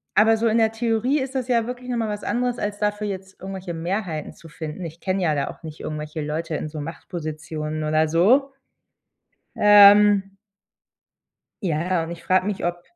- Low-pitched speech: No, high, 190 Hz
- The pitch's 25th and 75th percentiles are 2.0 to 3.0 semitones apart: No, wide, 5.5 semitones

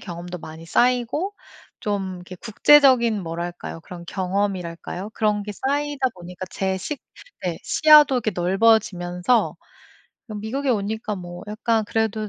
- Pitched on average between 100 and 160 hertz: No, high, 205 Hz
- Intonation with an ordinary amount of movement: Yes, average, 4.8 semitones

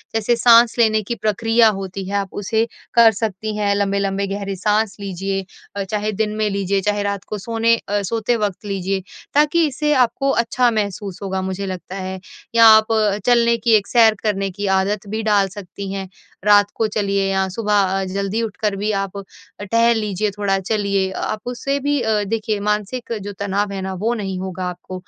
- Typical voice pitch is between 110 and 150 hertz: No, high, 205 Hz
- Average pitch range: No, narrow, 2.3 semitones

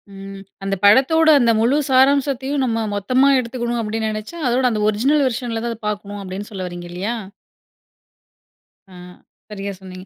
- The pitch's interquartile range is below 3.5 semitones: No, average, 4.3 semitones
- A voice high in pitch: Yes, high, 225 Hz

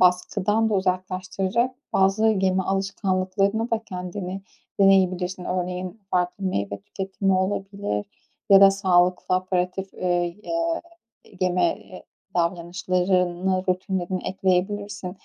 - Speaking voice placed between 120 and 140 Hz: No, medium, 185 Hz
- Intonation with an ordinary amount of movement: No, narrow, 1.4 semitones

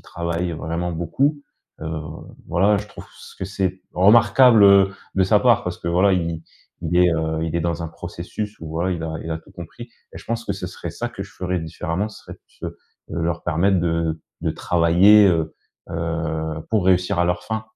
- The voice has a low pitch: Yes, very low, 85 Hz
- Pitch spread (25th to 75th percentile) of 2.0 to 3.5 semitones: Yes, average, 3.0 semitones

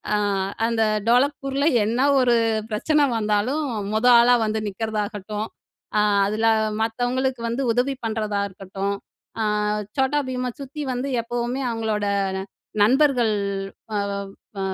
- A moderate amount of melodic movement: Yes, average, 3.5 semitones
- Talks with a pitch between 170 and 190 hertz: No, high, 230 Hz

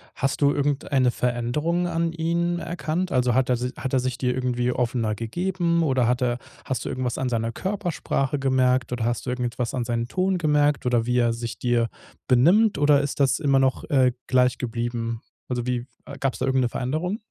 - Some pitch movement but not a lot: Yes, average, 3.5 semitones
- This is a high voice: No, low, 130 Hz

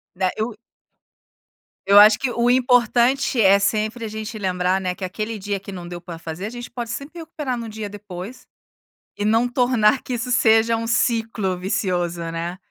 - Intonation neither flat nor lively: Yes, average, 4.0 semitones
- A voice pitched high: Yes, high, 215 Hz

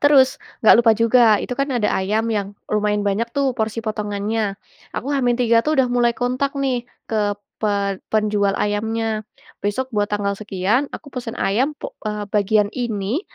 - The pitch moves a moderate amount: Yes, average, 3.2 semitones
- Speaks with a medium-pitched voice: No, high, 220 Hz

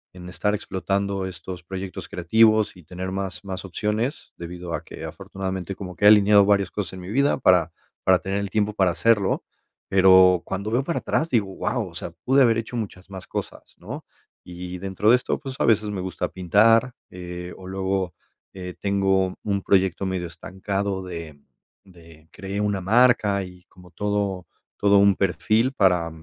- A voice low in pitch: Yes, very low, 95 Hz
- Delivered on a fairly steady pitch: Yes, narrow, 2.2 semitones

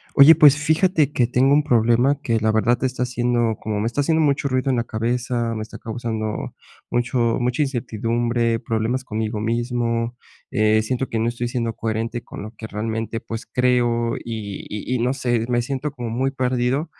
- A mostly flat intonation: Yes, narrow, 2.2 semitones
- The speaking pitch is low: Yes, low, 120 Hz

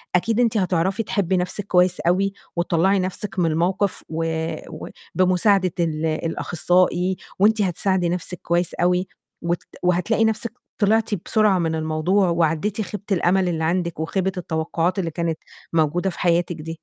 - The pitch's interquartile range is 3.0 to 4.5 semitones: No, narrow, 2.4 semitones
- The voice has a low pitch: No, medium, 180 Hz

